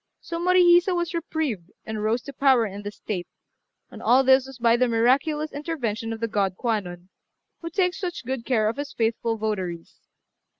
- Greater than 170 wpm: Yes, average, 180 wpm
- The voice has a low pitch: No, high, 240 Hz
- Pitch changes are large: Yes, wide, 6.1 semitones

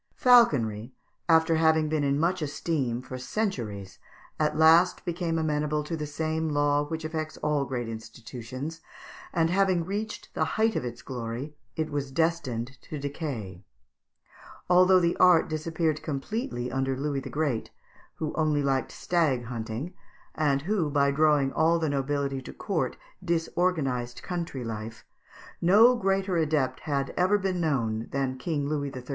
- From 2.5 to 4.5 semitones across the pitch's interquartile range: Yes, average, 3.9 semitones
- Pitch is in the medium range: Yes, medium, 150 Hz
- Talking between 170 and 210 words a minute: No, average, 150 wpm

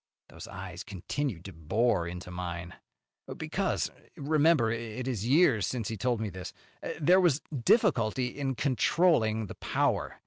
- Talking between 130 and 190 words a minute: Yes, average, 140 wpm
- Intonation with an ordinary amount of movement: No, wide, 7.0 semitones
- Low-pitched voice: Yes, low, 115 Hz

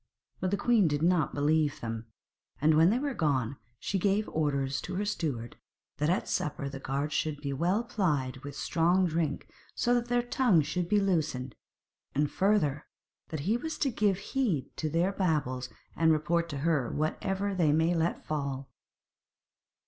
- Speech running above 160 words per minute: Yes, average, 170 wpm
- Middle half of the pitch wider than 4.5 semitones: Yes, average, 5.2 semitones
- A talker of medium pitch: Yes, medium, 160 Hz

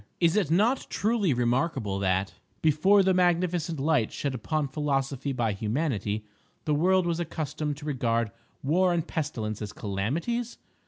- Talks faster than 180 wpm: No, average, 145 wpm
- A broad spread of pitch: Yes, wide, 6.6 semitones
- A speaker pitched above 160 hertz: No, medium, 150 Hz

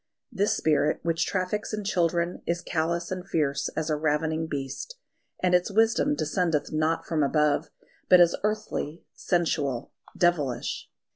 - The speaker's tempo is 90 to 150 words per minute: Yes, average, 140 wpm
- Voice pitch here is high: No, medium, 165 Hz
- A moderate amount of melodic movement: Yes, average, 3.2 semitones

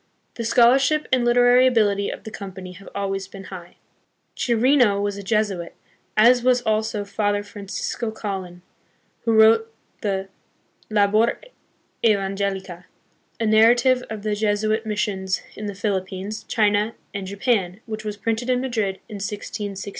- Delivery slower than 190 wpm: Yes, average, 145 wpm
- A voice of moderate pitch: No, high, 210 Hz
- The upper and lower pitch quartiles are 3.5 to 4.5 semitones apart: No, narrow, 2.4 semitones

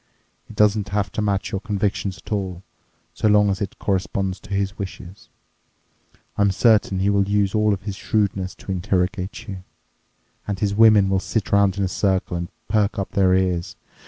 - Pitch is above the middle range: No, low, 100 Hz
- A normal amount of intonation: No, narrow, 1.5 semitones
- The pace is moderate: Yes, average, 180 wpm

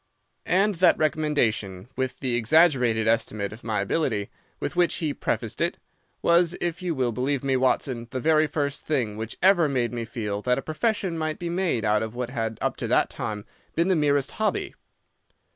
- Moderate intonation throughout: No, wide, 6.1 semitones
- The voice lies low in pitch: Yes, low, 130 Hz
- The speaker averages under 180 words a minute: No, average, 190 wpm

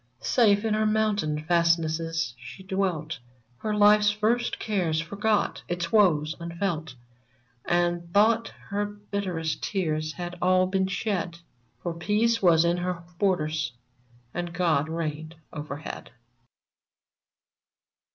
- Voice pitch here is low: No, medium, 175 Hz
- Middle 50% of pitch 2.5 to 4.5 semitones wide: Yes, average, 4.1 semitones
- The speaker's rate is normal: No, slow, 110 wpm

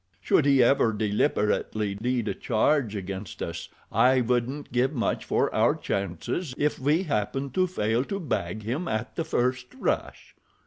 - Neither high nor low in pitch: No, low, 125 Hz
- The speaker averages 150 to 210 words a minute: Yes, average, 160 wpm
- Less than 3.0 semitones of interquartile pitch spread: No, average, 4.9 semitones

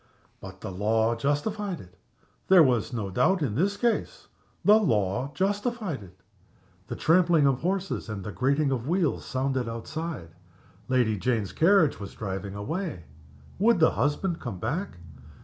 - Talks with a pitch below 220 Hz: Yes, low, 135 Hz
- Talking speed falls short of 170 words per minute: Yes, average, 150 wpm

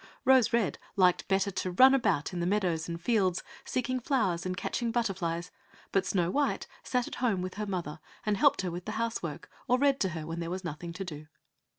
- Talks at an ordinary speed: No, fast, 220 wpm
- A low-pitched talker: No, high, 190 Hz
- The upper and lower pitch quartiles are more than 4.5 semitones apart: Yes, average, 5.1 semitones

